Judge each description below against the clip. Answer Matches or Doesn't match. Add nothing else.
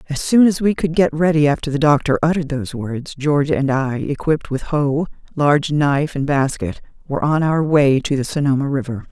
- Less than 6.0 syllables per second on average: Matches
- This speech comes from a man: Doesn't match